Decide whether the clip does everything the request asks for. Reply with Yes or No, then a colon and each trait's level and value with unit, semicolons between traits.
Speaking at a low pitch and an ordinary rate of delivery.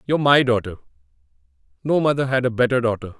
Yes: low, 130 Hz; average, 170 wpm